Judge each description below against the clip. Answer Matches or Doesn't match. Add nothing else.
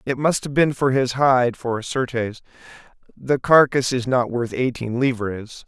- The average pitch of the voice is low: Matches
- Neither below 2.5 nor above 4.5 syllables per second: Matches